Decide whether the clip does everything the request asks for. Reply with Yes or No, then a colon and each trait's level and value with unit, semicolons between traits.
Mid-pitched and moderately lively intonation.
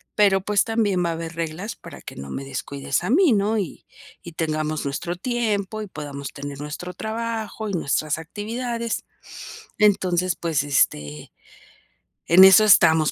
No: medium, 180 Hz; wide, 5.7 semitones